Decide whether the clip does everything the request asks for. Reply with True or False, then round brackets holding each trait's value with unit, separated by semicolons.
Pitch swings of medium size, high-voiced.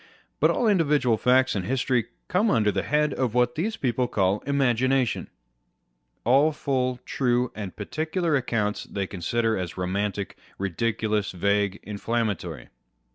False (4.7 semitones; 120 Hz)